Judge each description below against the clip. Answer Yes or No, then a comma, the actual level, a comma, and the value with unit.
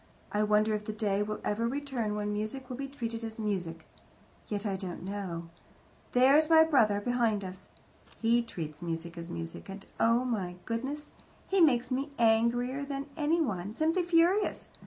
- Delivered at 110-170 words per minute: Yes, average, 165 wpm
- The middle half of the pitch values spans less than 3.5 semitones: No, average, 5.1 semitones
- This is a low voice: No, high, 225 Hz